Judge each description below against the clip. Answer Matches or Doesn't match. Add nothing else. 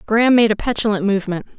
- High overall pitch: Matches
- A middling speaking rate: Matches